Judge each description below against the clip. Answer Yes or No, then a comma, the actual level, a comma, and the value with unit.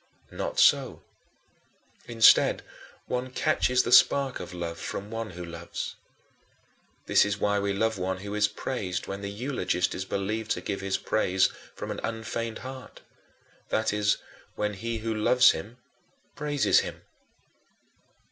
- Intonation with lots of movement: No, average, 3.1 semitones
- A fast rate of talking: No, average, 145 wpm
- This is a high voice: No, low, 105 Hz